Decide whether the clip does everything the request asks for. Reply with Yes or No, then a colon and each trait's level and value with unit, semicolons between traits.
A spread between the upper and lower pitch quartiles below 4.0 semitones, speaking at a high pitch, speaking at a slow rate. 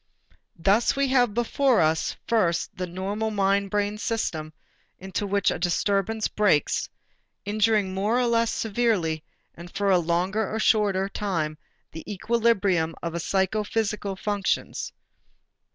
Yes: average, 3.5 semitones; high, 200 Hz; slow, 130 wpm